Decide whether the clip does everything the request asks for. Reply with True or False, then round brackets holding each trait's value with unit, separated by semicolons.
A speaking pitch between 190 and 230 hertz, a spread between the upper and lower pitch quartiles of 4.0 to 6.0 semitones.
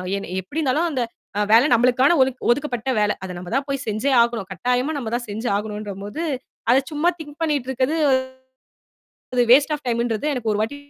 False (245 Hz; 4.5 semitones)